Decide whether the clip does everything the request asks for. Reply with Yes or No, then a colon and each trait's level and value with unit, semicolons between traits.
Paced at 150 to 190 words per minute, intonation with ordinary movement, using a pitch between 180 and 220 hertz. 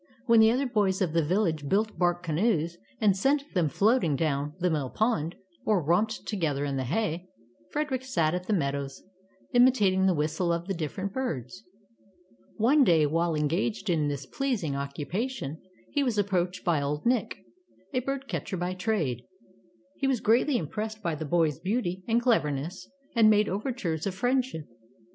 No: average, 170 wpm; wide, 6.1 semitones; medium, 185 Hz